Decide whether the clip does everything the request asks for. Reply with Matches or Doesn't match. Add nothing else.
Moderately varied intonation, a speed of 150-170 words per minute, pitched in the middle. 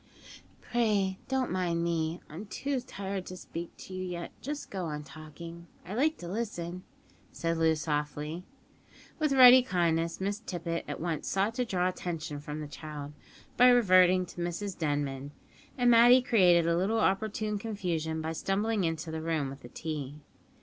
Matches